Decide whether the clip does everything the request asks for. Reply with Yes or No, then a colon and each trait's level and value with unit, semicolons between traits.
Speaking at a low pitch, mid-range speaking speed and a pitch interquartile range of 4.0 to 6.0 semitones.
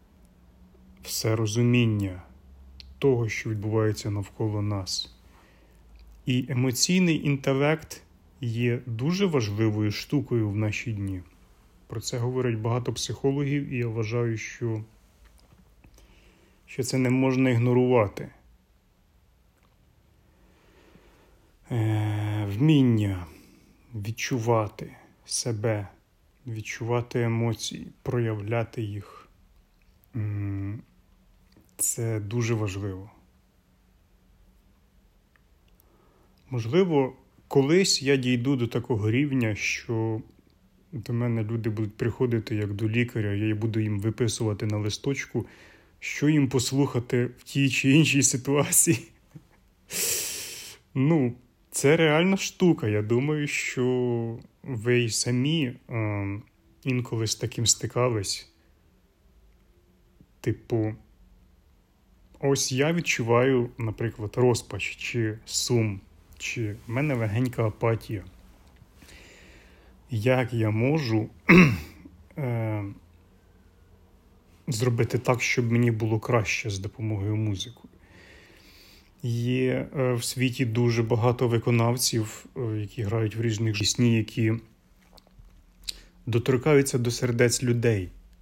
No: low, 115 Hz; slow, 85 wpm; average, 4.3 semitones